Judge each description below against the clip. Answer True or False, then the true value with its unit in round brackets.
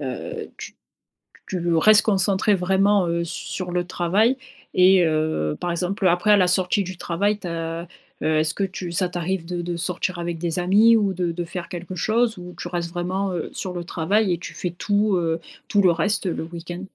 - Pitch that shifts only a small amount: True (2.3 semitones)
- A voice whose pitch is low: False (180 Hz)